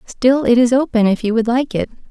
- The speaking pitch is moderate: No, high, 240 Hz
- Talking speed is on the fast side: Yes, fast, 255 wpm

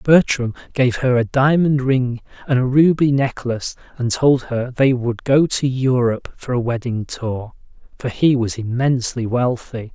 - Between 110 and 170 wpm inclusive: Yes, average, 165 wpm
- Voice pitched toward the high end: No, low, 125 Hz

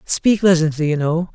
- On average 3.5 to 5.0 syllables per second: Yes, 4.8 syllables/s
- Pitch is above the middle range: No, medium, 165 Hz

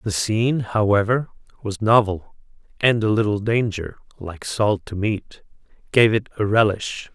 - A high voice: No, low, 105 Hz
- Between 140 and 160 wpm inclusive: Yes, average, 145 wpm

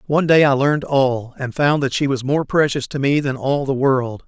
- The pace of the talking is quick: Yes, fast, 255 wpm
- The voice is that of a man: Yes, male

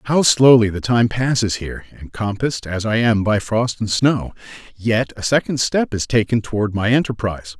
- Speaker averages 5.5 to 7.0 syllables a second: No, 5.0 syllables/s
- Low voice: Yes, low, 115 Hz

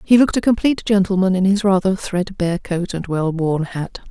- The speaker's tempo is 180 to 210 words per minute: Yes, fast, 205 wpm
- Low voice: No, high, 190 Hz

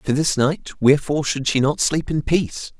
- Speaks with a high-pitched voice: No, medium, 145 Hz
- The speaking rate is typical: No, fast, 215 wpm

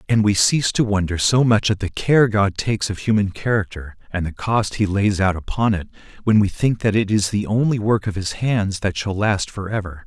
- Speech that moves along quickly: Yes, fast, 240 wpm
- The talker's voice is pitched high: No, low, 105 Hz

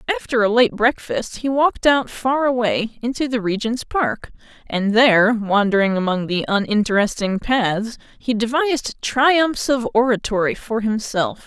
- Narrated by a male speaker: No, female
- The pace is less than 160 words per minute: Yes, average, 140 wpm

